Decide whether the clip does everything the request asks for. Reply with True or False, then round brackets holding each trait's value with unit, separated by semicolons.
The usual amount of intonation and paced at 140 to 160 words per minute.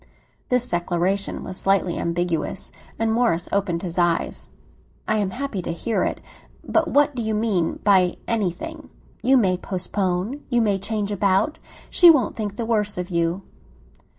True (4.3 semitones; 150 wpm)